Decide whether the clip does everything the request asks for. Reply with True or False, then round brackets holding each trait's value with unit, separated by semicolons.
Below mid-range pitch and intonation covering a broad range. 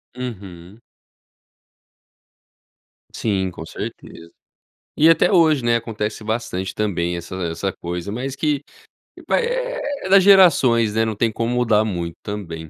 True (110 Hz; 6.3 semitones)